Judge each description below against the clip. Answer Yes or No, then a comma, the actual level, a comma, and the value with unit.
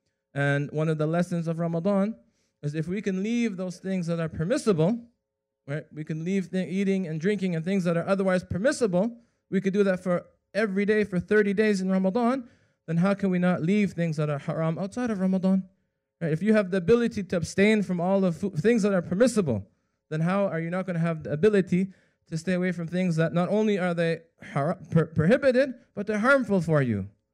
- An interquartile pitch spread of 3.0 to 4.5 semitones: Yes, average, 3.7 semitones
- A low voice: No, medium, 185 Hz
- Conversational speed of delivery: No, fast, 220 wpm